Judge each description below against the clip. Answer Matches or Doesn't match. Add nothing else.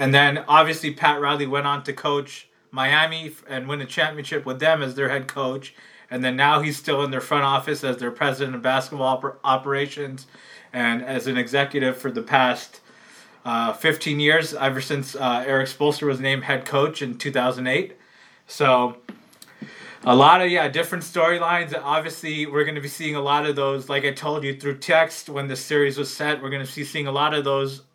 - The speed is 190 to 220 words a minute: Matches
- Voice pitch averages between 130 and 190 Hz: Matches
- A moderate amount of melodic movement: Doesn't match